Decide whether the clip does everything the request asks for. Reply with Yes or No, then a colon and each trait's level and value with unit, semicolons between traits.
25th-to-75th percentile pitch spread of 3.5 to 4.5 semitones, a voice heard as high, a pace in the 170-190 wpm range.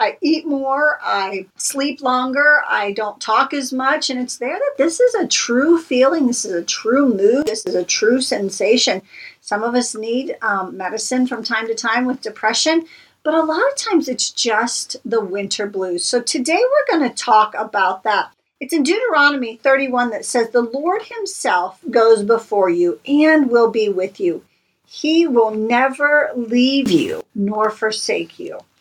No: average, 5.2 semitones; very high, 255 Hz; average, 175 wpm